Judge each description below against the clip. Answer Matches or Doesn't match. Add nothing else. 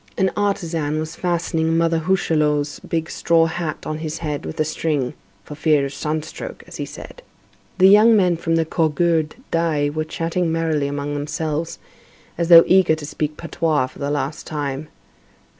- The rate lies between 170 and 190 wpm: Matches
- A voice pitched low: Doesn't match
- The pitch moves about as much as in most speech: Doesn't match